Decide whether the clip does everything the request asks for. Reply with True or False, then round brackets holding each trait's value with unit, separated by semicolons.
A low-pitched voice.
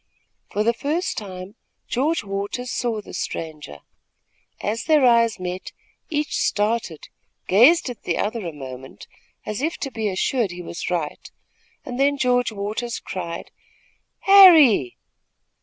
False (220 Hz)